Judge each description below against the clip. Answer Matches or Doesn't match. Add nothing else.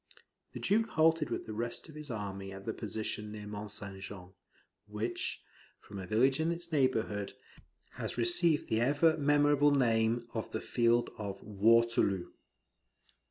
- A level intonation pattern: Doesn't match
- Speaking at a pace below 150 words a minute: Doesn't match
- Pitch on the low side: Matches